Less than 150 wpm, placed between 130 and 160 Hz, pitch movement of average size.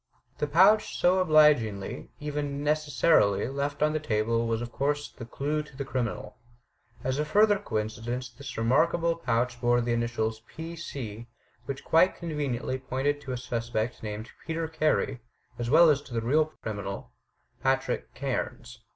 No: average, 155 wpm; low, 135 Hz; average, 4.5 semitones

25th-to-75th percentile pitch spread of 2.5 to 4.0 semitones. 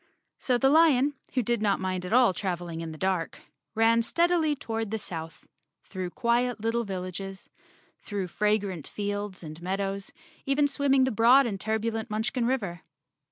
No: average, 4.7 semitones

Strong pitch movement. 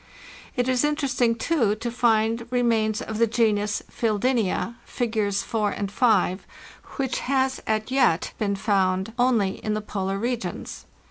No: average, 3.0 semitones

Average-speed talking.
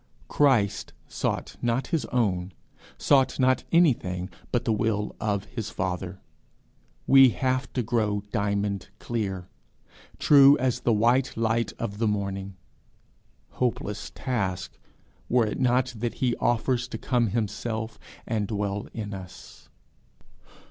No: slow, 125 wpm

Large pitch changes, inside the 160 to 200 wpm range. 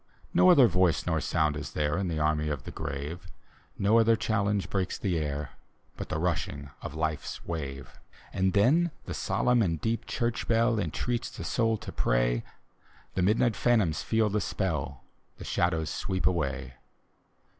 Yes: wide, 6.6 semitones; average, 165 wpm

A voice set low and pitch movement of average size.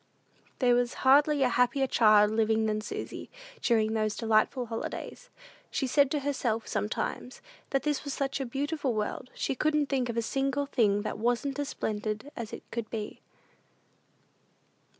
No: high, 245 Hz; average, 4.0 semitones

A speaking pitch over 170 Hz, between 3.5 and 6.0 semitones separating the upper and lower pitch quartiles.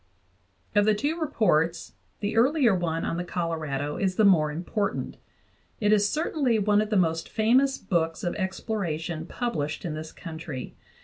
Yes: high, 190 Hz; average, 5.0 semitones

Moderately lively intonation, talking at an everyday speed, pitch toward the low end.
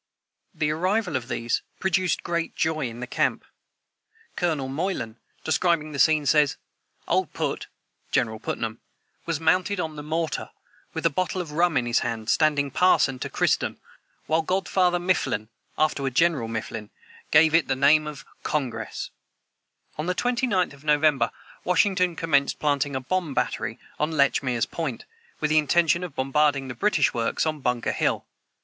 No: average, 4.2 semitones; average, 155 wpm; medium, 150 Hz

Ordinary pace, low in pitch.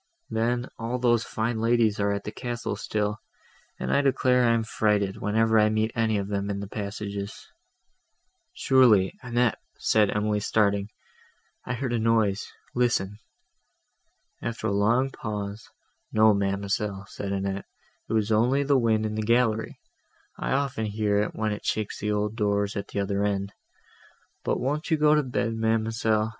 Yes: average, 165 wpm; low, 110 Hz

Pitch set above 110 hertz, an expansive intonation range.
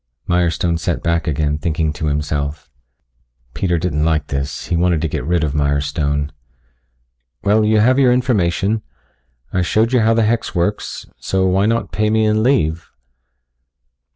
No: very low, 85 Hz; wide, 6.0 semitones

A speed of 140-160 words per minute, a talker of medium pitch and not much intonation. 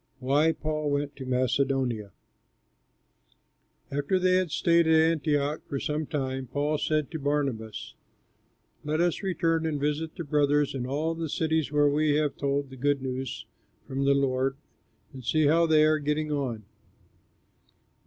Yes: average, 155 wpm; medium, 145 Hz; narrow, 2.3 semitones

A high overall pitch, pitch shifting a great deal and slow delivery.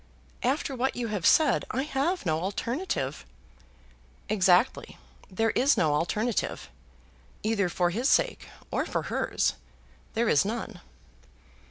Yes: high, 225 Hz; wide, 6.3 semitones; slow, 125 wpm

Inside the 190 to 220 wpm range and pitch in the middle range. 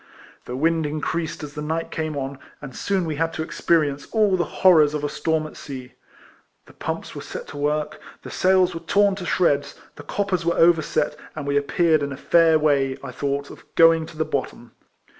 Yes: fast, 205 wpm; medium, 155 Hz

